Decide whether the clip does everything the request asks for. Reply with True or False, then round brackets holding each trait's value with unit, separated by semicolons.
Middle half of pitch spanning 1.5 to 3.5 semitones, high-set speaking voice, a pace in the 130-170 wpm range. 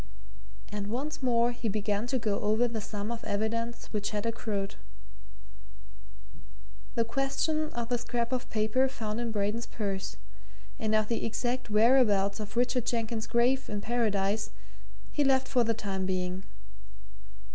True (2.7 semitones; 230 Hz; 145 wpm)